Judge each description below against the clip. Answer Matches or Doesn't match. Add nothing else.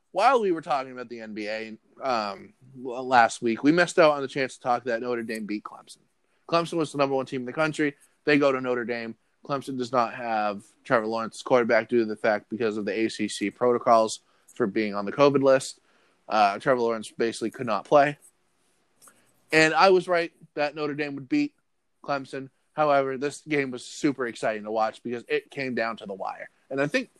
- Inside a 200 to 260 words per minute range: Matches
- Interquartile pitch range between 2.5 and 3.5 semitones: Doesn't match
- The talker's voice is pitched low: Matches